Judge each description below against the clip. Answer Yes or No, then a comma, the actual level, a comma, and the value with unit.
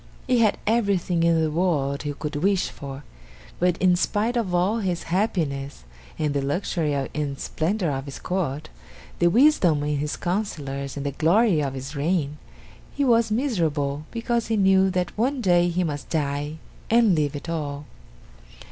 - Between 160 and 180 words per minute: Yes, average, 165 wpm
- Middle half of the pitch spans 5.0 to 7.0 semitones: Yes, wide, 5.4 semitones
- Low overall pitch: No, medium, 170 Hz